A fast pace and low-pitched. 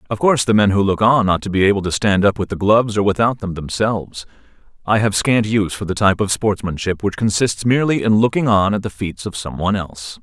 Yes: fast, 250 wpm; low, 100 Hz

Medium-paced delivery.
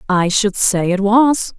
Yes: average, 190 wpm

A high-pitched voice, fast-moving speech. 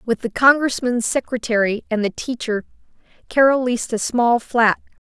No: high, 240 Hz; average, 140 wpm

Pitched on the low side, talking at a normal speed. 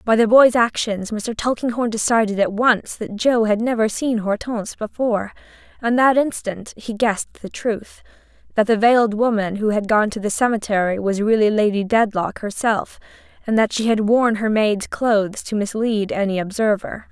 No: high, 220 Hz; average, 170 wpm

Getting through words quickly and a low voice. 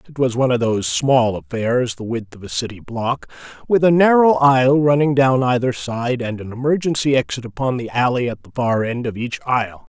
Yes: fast, 210 wpm; low, 125 Hz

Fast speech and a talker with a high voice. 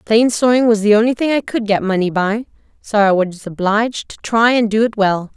Yes: fast, 235 wpm; high, 215 Hz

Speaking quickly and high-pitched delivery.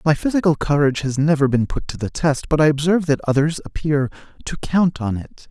No: fast, 220 wpm; medium, 150 Hz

